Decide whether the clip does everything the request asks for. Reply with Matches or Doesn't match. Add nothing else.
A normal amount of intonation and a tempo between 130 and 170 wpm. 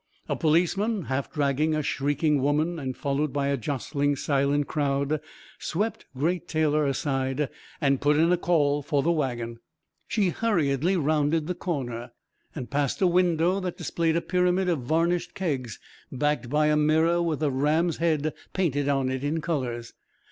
Matches